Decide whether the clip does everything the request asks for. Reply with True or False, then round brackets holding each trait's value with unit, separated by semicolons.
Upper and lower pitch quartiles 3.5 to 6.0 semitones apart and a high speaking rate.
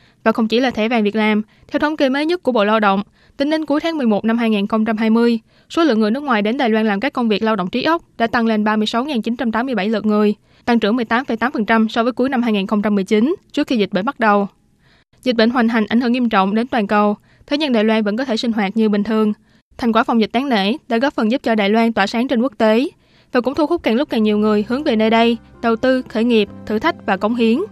False (2.7 semitones; 265 wpm)